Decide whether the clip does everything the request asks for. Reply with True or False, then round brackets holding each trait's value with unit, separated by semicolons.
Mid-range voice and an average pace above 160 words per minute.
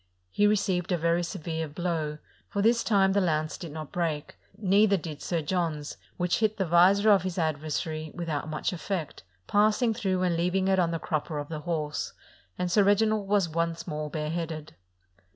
True (170 Hz; 190 wpm)